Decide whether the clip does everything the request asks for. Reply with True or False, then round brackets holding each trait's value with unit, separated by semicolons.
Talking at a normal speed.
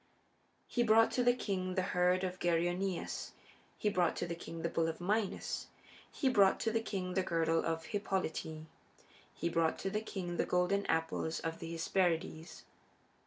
True (170 wpm)